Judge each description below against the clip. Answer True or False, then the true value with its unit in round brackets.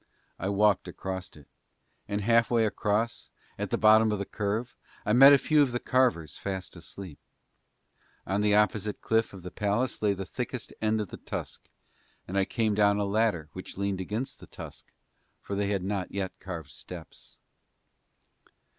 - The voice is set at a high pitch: False (105 Hz)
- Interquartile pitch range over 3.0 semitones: False (2.7 semitones)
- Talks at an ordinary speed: True (175 wpm)